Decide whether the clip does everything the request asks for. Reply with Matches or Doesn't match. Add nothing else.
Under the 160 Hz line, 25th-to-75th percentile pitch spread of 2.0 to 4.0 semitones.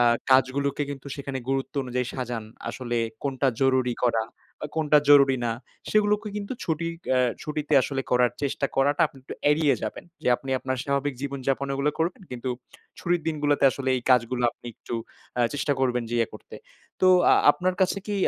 Matches